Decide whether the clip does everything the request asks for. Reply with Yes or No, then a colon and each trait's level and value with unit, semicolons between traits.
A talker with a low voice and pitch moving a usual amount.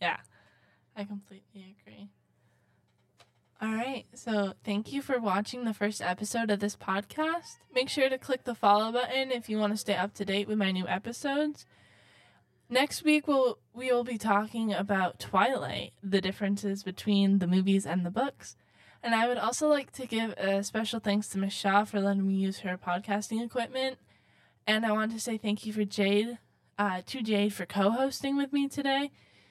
No: high, 210 Hz; average, 3.9 semitones